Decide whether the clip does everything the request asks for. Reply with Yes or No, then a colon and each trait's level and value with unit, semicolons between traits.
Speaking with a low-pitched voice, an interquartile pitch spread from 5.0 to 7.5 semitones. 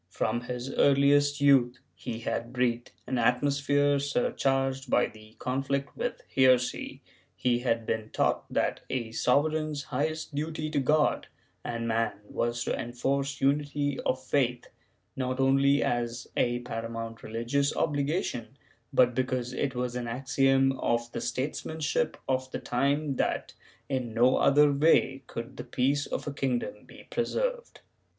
No: low, 130 Hz; average, 2.8 semitones